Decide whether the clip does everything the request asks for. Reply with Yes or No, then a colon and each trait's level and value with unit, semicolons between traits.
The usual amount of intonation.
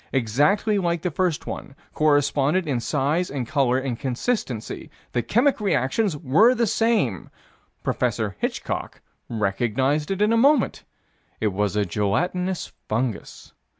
No: wide, 7.8 semitones